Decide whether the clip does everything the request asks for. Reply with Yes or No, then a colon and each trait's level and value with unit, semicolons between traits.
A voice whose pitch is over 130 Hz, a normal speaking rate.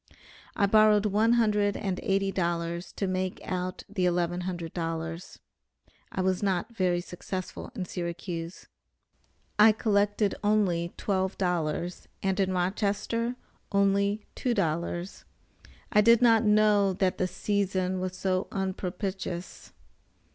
No: high, 190 Hz; slow, 125 wpm